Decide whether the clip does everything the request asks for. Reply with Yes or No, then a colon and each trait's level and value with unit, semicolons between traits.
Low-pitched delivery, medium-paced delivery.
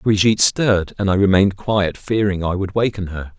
Yes: low, 100 Hz; average, 195 wpm